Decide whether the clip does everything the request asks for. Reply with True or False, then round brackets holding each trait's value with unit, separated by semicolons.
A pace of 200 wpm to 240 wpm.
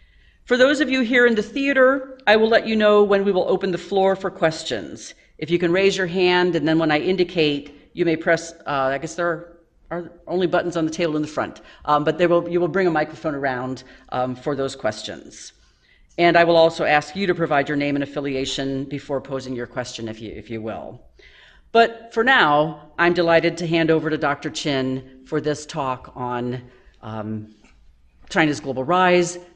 True (205 wpm)